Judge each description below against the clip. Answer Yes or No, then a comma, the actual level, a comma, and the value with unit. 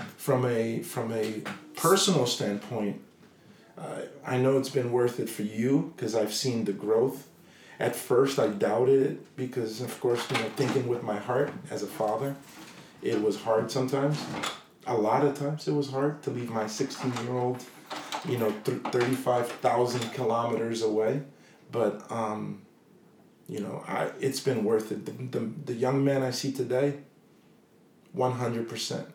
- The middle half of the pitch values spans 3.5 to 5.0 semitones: No, average, 3.1 semitones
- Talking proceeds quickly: No, average, 160 wpm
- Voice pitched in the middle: No, low, 125 Hz